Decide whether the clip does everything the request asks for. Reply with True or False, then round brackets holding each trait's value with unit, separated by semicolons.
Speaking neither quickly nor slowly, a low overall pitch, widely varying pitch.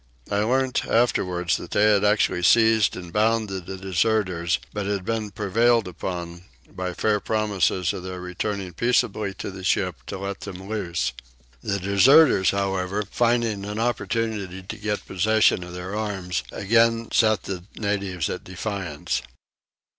False (145 wpm; 100 Hz; 3.0 semitones)